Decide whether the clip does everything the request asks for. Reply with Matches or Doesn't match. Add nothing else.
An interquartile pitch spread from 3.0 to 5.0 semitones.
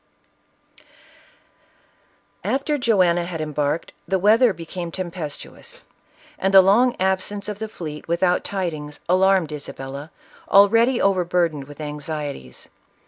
Matches